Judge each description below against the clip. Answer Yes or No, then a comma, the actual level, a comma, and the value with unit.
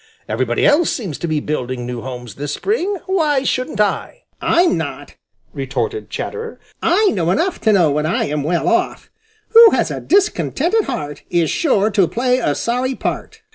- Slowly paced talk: No, average, 175 wpm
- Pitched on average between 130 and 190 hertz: No, high, 220 Hz